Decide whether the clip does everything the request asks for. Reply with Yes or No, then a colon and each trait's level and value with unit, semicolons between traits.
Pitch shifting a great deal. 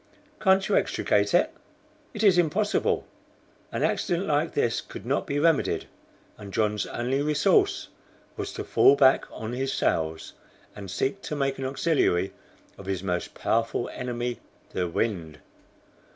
Yes: wide, 6.8 semitones